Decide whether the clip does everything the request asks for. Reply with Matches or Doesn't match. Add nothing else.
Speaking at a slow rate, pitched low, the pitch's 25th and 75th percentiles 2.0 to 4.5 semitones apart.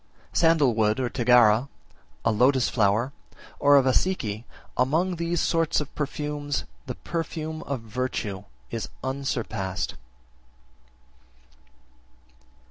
Doesn't match